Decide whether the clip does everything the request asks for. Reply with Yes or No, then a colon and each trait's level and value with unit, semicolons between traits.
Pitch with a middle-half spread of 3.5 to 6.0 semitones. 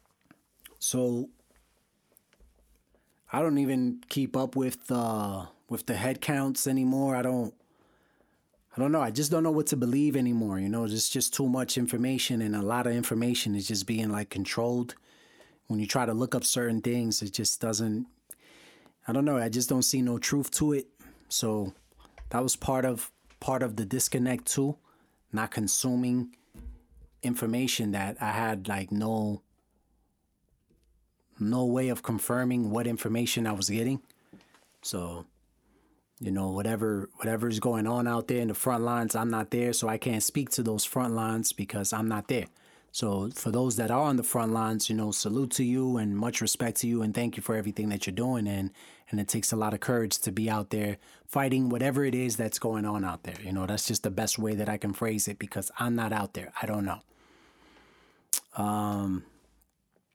No: average, 3.0 semitones